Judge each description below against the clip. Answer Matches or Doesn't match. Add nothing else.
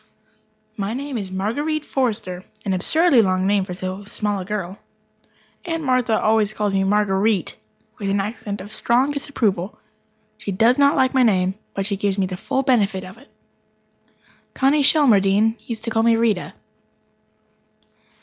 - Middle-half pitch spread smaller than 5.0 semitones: Matches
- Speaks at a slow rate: Doesn't match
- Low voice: Doesn't match